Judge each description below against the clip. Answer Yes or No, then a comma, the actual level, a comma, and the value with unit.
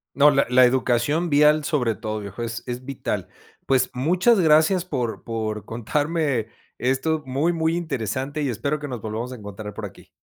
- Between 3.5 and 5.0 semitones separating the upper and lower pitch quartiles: Yes, average, 4.7 semitones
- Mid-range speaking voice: No, low, 130 Hz